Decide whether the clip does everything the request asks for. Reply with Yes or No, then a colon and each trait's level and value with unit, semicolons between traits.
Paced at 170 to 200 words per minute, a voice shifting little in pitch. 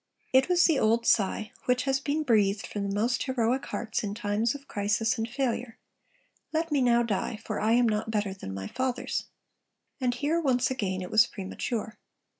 No: average, 190 wpm; average, 3.7 semitones